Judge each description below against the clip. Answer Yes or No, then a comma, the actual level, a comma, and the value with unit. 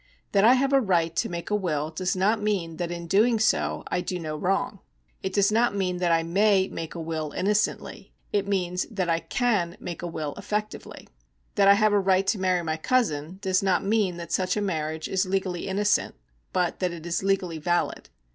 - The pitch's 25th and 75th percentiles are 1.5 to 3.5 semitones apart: Yes, average, 3.1 semitones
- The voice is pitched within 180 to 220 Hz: Yes, medium, 185 Hz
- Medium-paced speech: No, fast, 215 wpm